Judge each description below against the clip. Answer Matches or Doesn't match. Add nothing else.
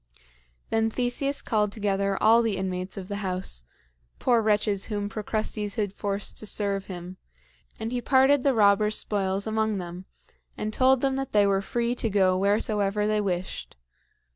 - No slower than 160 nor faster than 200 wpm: Matches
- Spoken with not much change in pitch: Matches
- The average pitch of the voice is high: Matches